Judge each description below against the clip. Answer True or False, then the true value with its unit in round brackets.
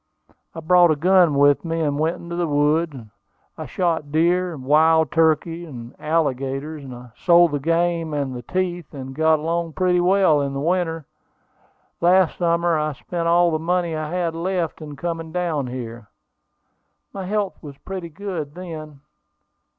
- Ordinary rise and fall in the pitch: True (3.0 semitones)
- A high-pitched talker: False (165 Hz)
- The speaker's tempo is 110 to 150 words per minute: False (160 wpm)